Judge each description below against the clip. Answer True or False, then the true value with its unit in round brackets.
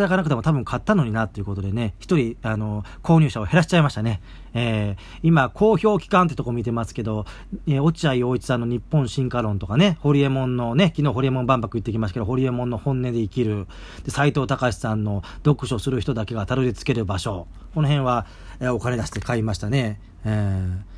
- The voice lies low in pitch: True (120 Hz)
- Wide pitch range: False (4.8 semitones)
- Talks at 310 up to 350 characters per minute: False (430 characters per minute)